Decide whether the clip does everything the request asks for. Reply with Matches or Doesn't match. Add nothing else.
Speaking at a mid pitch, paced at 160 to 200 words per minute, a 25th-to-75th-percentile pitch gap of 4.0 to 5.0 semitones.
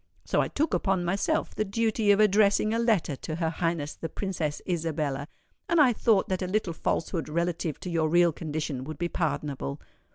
Matches